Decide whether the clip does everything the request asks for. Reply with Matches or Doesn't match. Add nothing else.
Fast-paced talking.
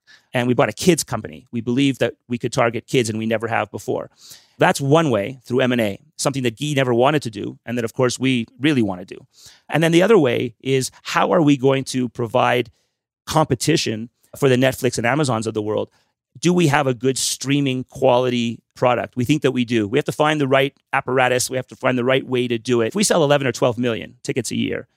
Matches